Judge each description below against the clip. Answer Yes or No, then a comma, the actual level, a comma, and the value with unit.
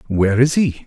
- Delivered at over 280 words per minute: No, fast, 210 wpm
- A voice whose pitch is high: No, low, 125 Hz